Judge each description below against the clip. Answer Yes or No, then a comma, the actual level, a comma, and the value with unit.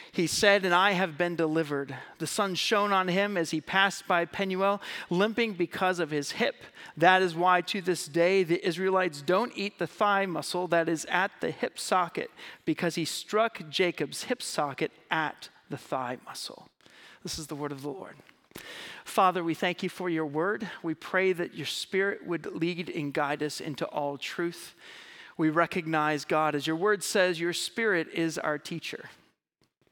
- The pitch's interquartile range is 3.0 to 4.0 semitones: Yes, average, 3.5 semitones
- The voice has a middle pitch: Yes, medium, 175 Hz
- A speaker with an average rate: Yes, average, 180 wpm